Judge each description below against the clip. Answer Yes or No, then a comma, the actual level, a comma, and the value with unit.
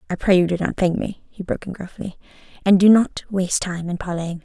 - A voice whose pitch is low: No, medium, 185 Hz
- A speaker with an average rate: No, fast, 245 wpm